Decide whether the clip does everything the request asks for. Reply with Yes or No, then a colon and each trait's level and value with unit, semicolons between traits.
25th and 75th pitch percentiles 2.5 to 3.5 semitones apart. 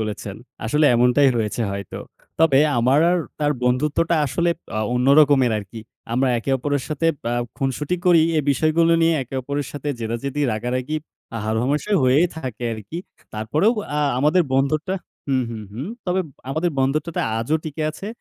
No: average, 4.3 semitones